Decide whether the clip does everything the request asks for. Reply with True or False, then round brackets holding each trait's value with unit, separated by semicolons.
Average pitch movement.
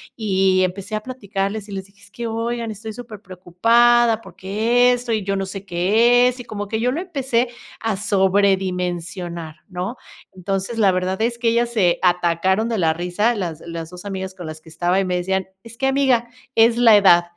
True (4.1 semitones)